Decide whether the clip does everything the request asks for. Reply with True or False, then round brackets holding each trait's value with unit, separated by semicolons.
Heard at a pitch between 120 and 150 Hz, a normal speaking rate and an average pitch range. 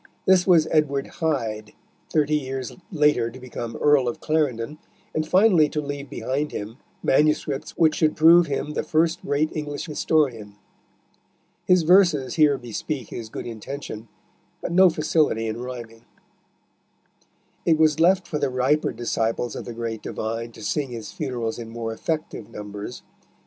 True (140 Hz; 150 wpm; 5.0 semitones)